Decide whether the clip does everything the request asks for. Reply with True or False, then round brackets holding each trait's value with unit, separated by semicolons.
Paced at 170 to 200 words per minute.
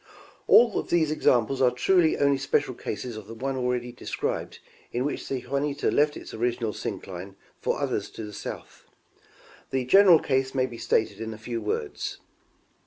True (175 wpm)